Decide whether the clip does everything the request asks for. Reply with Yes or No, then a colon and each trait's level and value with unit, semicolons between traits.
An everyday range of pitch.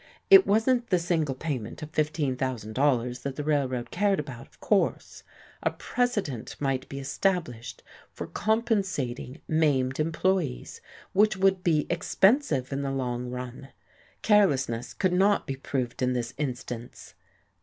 No: wide, 6.9 semitones